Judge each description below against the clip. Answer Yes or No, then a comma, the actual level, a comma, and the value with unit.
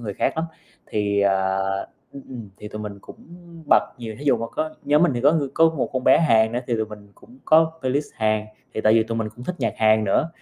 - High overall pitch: No, low, 115 Hz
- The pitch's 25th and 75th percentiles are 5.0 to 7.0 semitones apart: Yes, average, 5.3 semitones